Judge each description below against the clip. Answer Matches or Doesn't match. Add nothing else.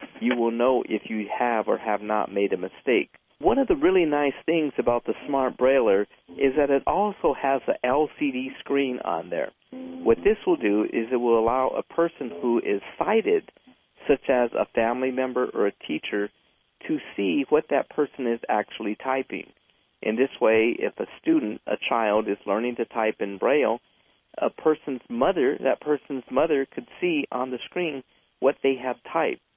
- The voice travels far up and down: Matches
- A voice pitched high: Doesn't match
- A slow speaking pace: Doesn't match